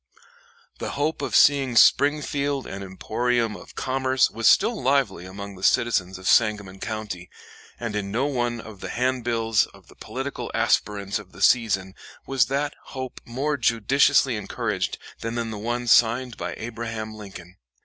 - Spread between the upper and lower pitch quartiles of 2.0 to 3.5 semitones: No, average, 3.9 semitones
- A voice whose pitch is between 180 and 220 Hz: No, low, 115 Hz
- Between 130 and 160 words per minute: Yes, average, 155 wpm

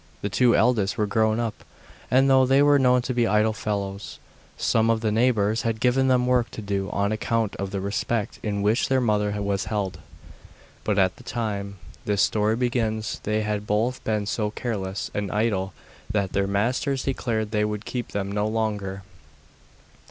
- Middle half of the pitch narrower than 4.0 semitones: Yes, narrow, 2.6 semitones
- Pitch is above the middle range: No, low, 110 Hz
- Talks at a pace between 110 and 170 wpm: No, average, 180 wpm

